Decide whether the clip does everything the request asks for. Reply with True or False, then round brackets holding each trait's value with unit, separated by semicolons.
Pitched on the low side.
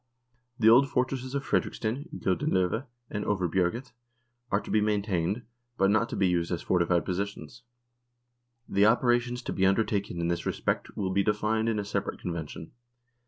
True (105 Hz)